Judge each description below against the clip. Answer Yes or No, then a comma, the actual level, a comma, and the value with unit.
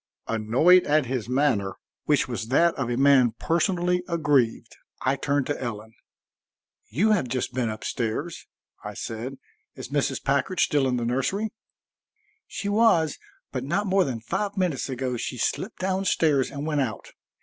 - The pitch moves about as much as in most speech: No, wide, 5.8 semitones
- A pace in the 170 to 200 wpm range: No, average, 160 wpm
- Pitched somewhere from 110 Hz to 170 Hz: Yes, medium, 140 Hz